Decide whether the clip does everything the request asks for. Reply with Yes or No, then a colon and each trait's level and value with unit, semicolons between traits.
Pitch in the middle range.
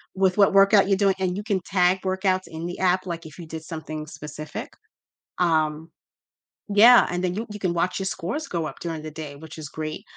Yes: medium, 180 Hz